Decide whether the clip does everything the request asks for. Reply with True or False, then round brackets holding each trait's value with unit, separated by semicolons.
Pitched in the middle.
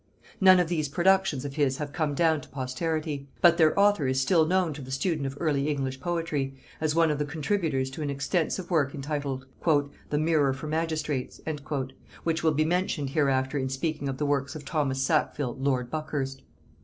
True (150 Hz)